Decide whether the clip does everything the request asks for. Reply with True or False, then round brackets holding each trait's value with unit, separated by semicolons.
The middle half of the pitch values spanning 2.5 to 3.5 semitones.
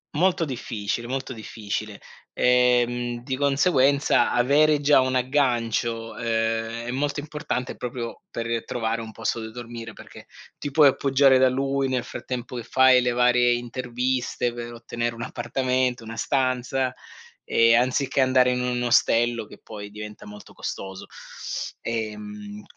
False (2.1 semitones)